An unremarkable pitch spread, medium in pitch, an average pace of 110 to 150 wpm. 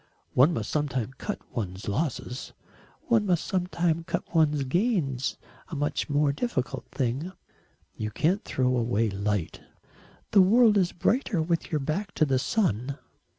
No: wide, 6.1 semitones; medium, 150 Hz; average, 145 wpm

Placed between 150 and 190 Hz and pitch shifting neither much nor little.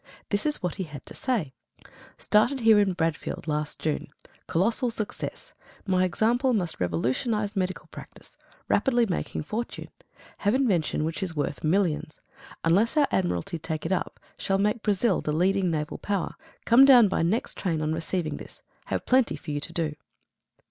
No: medium, 185 Hz; wide, 5.7 semitones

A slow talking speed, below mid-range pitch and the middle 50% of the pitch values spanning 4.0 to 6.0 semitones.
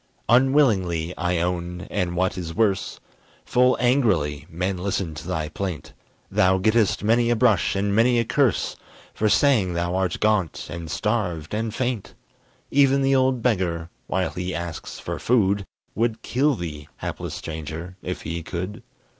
No: average, 155 wpm; very low, 95 Hz; average, 5.3 semitones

